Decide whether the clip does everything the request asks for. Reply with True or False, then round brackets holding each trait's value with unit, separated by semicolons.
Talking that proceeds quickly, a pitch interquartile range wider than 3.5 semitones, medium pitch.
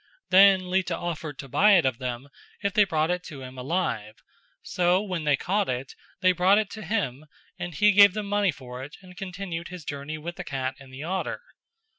True (210 wpm; 5.5 semitones; 175 Hz)